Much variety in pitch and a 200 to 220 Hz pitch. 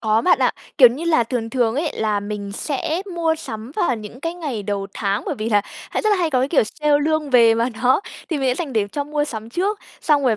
No: wide, 6.0 semitones; very high, 255 Hz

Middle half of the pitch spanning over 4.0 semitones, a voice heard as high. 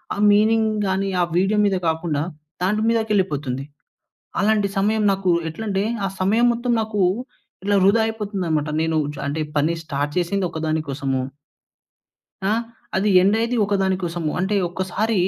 Yes: average, 4.7 semitones; high, 195 Hz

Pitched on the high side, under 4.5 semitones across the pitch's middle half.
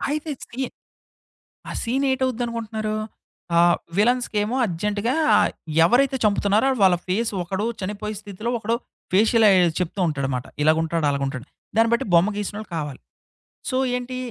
No: high, 210 Hz; average, 5.1 semitones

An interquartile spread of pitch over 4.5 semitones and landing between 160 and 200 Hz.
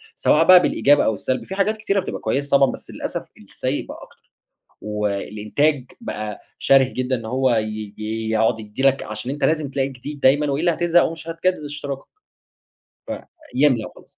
No: wide, 5.5 semitones; low, 135 Hz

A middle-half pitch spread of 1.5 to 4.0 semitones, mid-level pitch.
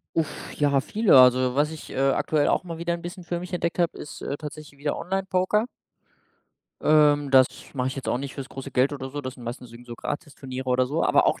No: average, 4.5 semitones; medium, 145 Hz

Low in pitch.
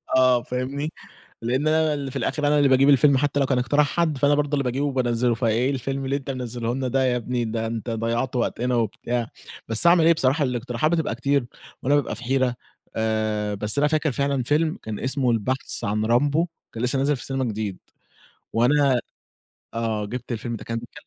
Yes: low, 130 Hz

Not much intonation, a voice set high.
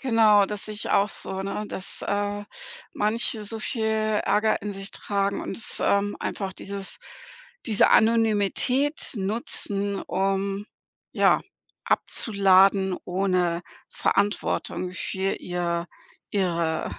Yes: narrow, 1.8 semitones; high, 200 Hz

